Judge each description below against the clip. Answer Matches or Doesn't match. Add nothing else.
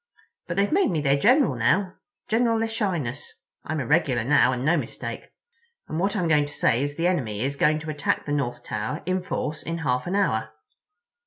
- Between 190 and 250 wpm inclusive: Matches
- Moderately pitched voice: Matches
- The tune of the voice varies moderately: Doesn't match